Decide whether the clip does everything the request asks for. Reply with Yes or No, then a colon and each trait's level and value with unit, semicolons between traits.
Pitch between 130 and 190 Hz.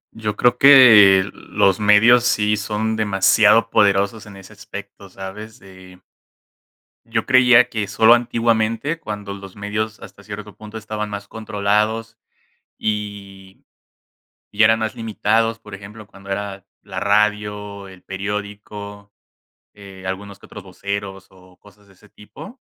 No: low, 105 Hz